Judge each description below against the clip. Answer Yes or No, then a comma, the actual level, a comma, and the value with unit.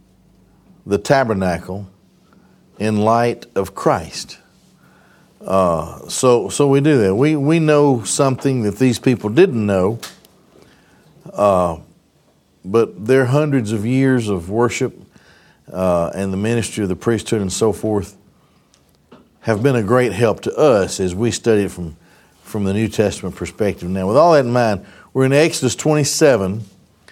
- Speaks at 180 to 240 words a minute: No, average, 145 wpm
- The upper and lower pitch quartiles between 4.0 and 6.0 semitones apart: Yes, average, 5.0 semitones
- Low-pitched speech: Yes, low, 110 Hz